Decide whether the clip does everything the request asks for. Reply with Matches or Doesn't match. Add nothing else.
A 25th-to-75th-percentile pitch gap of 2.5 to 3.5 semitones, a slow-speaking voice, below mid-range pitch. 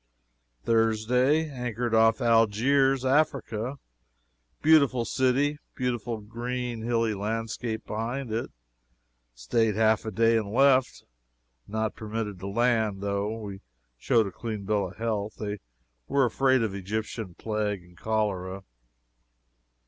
Matches